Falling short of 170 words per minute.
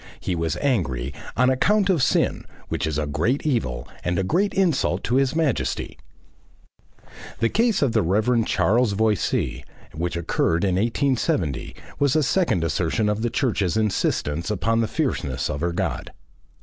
Yes: average, 160 wpm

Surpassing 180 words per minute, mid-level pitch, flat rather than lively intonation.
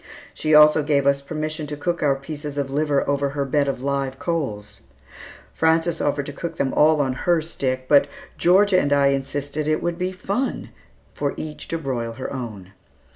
Yes: average, 190 wpm; medium, 145 Hz; narrow, 2.3 semitones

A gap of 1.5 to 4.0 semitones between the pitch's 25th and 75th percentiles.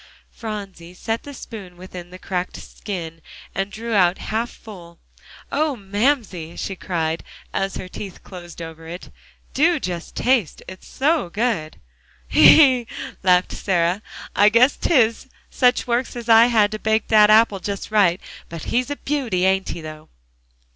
No: average, 4.7 semitones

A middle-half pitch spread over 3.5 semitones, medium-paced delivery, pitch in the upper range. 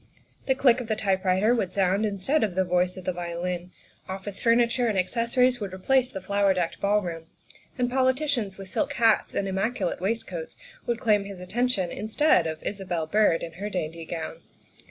Yes: average, 4.3 semitones; average, 180 wpm; high, 200 Hz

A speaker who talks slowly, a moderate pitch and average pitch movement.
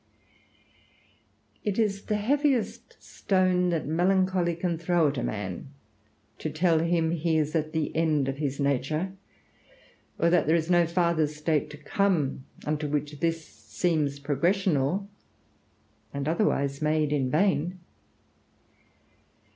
Yes: slow, 130 wpm; medium, 160 Hz; average, 3.4 semitones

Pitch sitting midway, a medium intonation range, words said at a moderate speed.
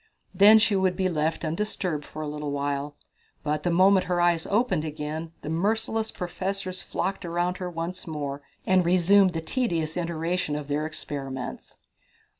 Yes: medium, 170 Hz; average, 3.6 semitones; average, 160 wpm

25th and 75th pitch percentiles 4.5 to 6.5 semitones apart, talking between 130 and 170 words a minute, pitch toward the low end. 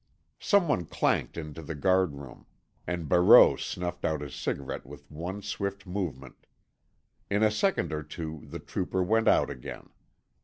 Yes: average, 4.8 semitones; average, 150 wpm; very low, 85 Hz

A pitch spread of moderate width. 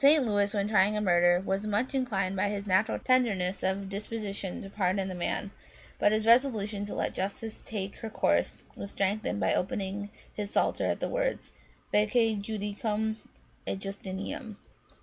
No: narrow, 2.0 semitones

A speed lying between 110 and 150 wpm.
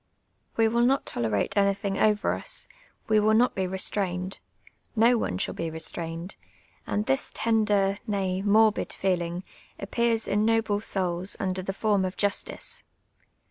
Yes: average, 140 wpm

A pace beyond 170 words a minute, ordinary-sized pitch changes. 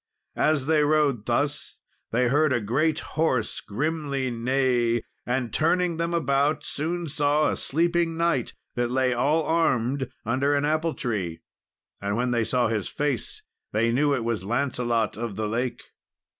No: average, 155 wpm; average, 4.4 semitones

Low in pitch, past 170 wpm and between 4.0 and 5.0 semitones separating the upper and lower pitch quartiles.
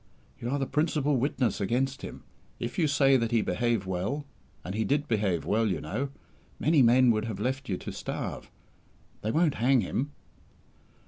Yes: low, 120 Hz; average, 180 wpm; average, 4.5 semitones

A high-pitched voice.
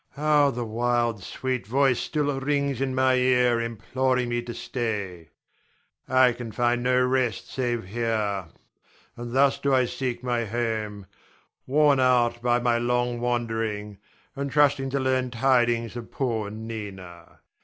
No: low, 120 Hz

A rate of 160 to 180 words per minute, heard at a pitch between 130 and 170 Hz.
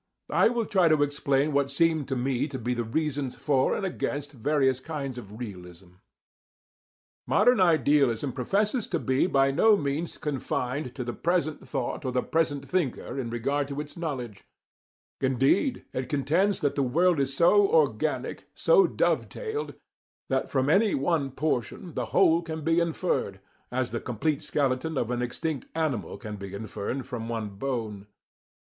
Yes: average, 165 wpm; medium, 140 Hz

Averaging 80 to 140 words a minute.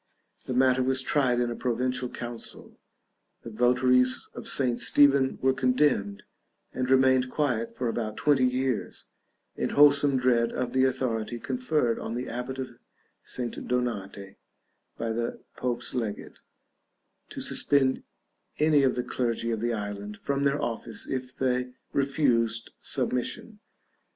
Yes: slow, 135 wpm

